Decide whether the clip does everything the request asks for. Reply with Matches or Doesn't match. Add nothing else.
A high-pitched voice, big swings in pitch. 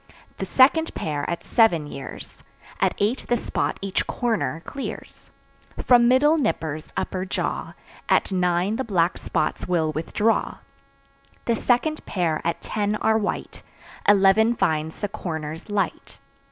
Matches